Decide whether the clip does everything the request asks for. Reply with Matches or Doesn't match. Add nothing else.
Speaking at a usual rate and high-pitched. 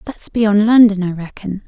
Matches